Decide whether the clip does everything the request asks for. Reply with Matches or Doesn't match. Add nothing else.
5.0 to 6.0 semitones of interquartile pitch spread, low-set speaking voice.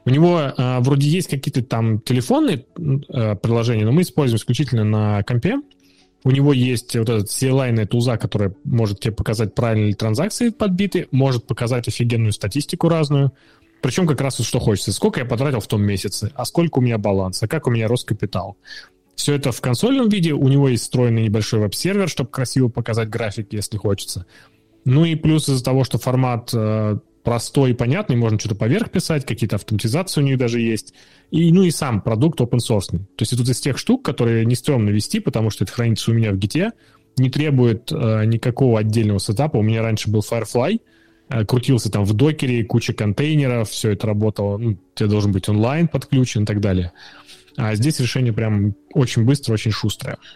Doesn't match